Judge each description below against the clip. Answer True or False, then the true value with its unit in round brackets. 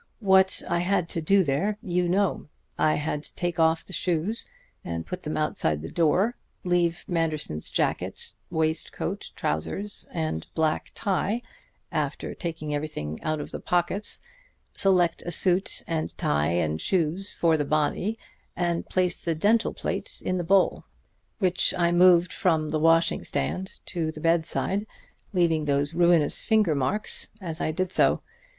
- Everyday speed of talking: True (155 wpm)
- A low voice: False (170 Hz)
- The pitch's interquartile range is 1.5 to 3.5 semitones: True (3.1 semitones)